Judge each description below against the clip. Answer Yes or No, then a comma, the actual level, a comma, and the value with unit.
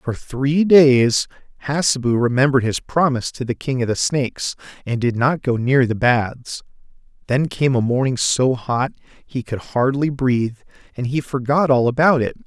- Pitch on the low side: Yes, low, 130 Hz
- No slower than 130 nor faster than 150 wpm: No, average, 175 wpm